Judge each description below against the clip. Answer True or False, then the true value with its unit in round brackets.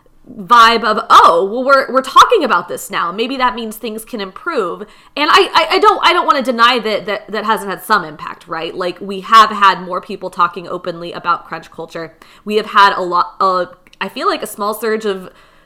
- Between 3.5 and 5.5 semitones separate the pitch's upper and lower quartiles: True (4.5 semitones)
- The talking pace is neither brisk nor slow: False (220 wpm)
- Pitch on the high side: True (210 Hz)